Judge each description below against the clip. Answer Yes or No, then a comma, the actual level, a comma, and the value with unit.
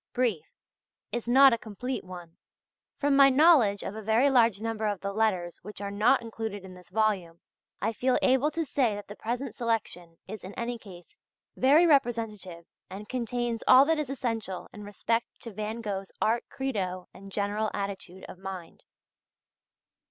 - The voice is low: No, high, 220 Hz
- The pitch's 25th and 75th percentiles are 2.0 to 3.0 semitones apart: No, average, 4.0 semitones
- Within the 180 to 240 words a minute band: No, average, 170 wpm